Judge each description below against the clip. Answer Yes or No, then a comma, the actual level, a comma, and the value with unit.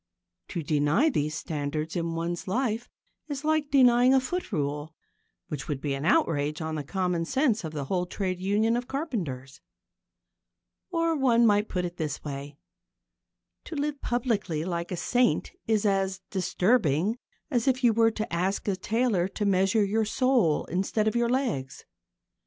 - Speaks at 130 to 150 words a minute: No, average, 165 wpm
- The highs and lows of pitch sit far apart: Yes, wide, 7.1 semitones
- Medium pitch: No, high, 195 Hz